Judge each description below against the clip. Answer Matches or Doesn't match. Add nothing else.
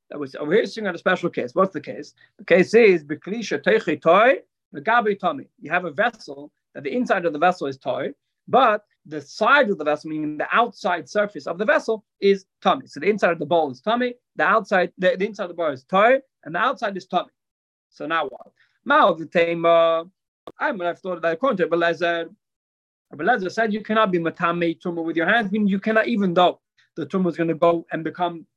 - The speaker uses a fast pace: Matches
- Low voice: Doesn't match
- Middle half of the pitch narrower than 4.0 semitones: Doesn't match